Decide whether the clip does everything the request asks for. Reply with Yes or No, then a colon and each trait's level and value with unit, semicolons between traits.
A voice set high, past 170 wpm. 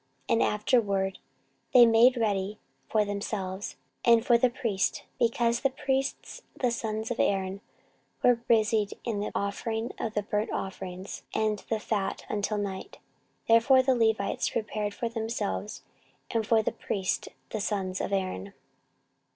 No: high, 215 Hz; average, 140 wpm